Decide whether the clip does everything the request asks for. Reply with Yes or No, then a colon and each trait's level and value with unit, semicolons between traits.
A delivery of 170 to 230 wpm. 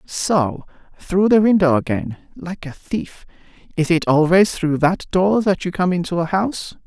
No: average, 150 wpm